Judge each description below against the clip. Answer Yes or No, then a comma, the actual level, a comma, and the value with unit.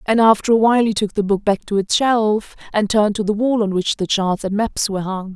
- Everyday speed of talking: No, fast, 280 wpm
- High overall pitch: Yes, high, 210 Hz